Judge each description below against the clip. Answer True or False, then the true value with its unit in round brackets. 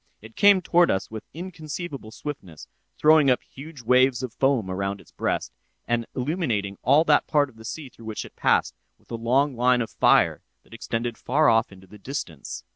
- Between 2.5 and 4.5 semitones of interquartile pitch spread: False (4.9 semitones)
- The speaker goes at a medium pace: True (195 wpm)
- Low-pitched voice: True (125 Hz)